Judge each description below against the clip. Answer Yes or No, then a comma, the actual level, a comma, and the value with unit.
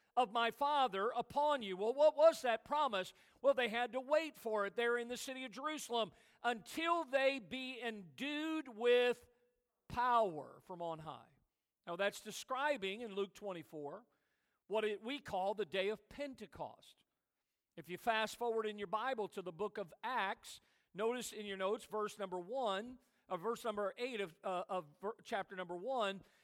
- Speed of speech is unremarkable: Yes, average, 170 wpm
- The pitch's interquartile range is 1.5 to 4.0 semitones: No, average, 4.4 semitones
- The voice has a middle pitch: No, high, 225 Hz